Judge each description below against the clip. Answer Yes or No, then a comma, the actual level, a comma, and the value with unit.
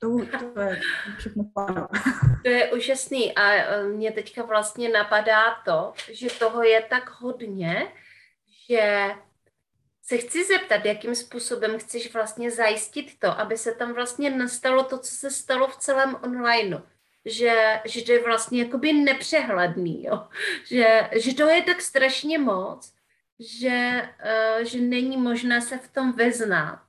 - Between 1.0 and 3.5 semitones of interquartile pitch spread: Yes, average, 2.8 semitones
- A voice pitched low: No, high, 235 Hz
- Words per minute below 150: Yes, average, 135 wpm